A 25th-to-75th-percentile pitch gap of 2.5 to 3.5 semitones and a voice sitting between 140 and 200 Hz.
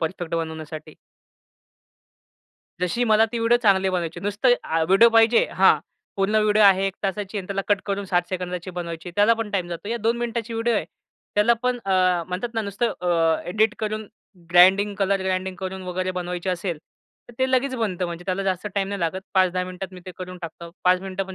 Yes: average, 2.9 semitones; high, 190 Hz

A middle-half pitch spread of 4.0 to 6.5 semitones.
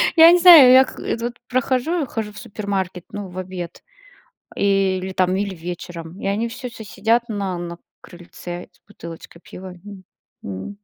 Yes: average, 4.6 semitones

